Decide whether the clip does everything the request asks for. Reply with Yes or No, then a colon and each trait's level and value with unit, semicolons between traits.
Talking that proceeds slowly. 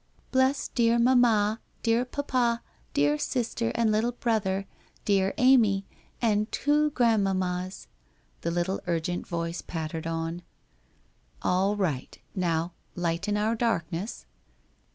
Yes: slow, 125 wpm